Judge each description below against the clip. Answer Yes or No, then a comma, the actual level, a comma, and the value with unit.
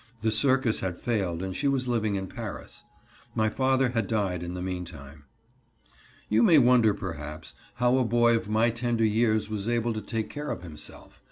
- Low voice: Yes, low, 110 Hz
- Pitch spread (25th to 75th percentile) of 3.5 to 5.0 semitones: Yes, average, 4.2 semitones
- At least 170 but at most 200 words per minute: Yes, average, 185 wpm